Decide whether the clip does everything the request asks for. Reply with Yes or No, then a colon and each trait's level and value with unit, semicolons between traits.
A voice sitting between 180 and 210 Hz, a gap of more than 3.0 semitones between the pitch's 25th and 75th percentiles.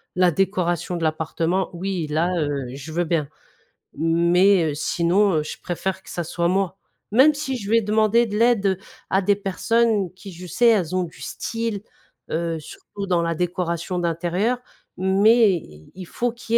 Yes: medium, 185 Hz; average, 3.5 semitones